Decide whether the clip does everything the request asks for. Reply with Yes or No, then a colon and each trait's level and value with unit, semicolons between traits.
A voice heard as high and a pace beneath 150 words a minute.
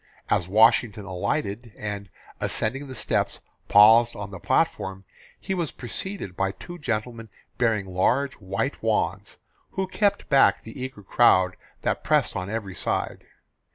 No: low, 110 Hz; average, 140 wpm